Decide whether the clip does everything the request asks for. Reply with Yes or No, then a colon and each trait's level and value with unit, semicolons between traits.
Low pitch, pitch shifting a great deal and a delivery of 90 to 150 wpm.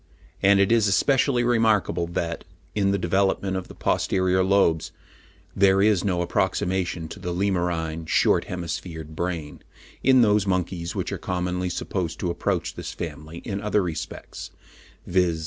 No: very low, 90 Hz; narrow, 2.6 semitones; average, 145 wpm